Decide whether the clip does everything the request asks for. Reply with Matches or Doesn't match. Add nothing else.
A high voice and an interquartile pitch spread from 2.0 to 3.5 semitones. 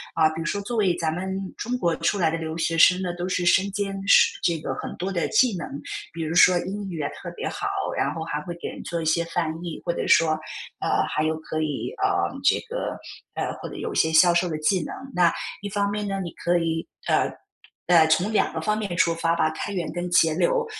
Doesn't match